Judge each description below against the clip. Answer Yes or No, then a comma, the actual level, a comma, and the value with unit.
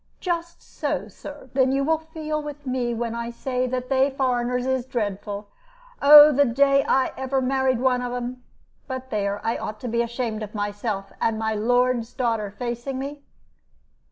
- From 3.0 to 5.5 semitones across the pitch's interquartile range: No, narrow, 2.6 semitones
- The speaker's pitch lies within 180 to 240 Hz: No, very high, 250 Hz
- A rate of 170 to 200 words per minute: Yes, average, 180 wpm